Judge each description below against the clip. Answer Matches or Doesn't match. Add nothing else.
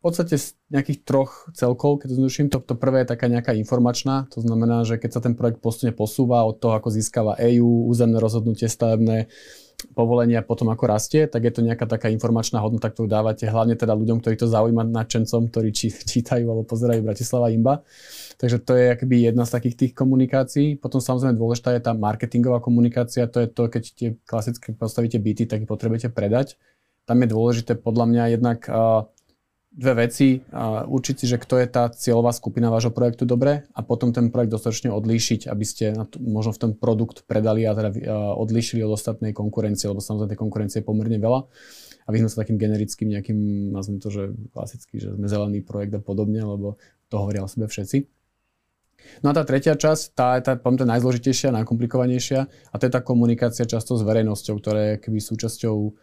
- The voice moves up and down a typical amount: Doesn't match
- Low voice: Matches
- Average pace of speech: Doesn't match